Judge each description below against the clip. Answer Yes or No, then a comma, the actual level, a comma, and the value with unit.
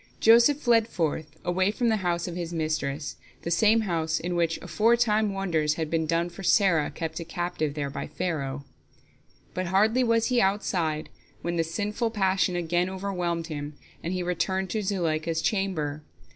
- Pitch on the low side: No, medium, 175 Hz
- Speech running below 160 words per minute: No, average, 170 wpm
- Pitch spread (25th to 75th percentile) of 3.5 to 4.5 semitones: Yes, average, 3.8 semitones